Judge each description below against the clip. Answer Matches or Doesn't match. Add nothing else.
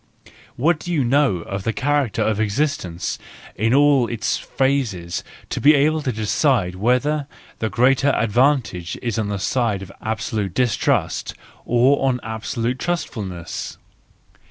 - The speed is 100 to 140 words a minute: Matches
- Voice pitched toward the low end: Matches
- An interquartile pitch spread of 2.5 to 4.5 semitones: Doesn't match